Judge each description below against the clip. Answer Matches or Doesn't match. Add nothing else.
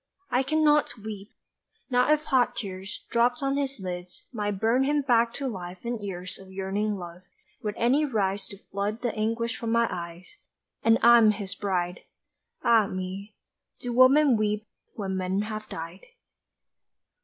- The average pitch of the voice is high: Matches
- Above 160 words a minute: Doesn't match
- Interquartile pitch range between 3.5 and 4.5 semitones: Matches